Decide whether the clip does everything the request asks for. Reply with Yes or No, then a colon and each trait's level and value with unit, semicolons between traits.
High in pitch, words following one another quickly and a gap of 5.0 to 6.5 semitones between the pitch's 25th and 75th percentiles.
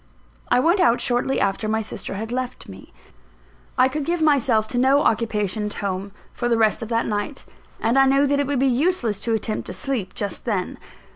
No: high, 240 Hz; fast, 210 wpm; average, 4.1 semitones